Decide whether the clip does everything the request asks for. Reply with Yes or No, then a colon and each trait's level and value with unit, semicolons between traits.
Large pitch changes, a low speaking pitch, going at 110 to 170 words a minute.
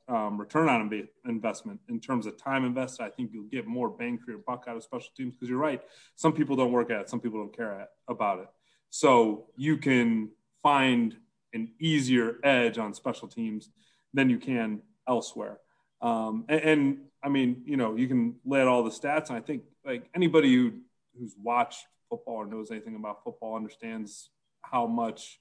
No: wide, 6.1 semitones; low, 130 Hz; average, 195 wpm